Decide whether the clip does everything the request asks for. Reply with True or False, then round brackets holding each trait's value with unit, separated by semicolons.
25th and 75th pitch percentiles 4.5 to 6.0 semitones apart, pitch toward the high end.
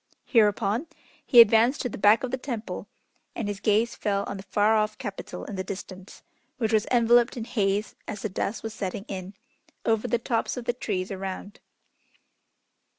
False (2.9 semitones; 215 Hz)